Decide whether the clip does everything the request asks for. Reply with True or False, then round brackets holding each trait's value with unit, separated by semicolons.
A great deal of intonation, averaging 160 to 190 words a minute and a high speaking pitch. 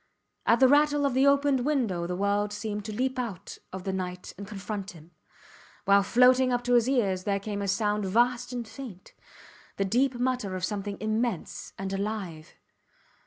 False (4.2 semitones; 180 wpm; 210 Hz)